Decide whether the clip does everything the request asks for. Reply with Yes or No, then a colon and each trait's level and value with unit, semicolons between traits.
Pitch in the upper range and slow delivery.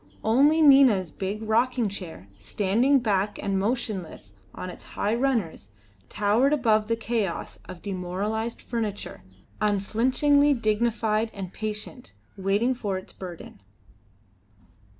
Yes: high, 215 Hz; slow, 110 wpm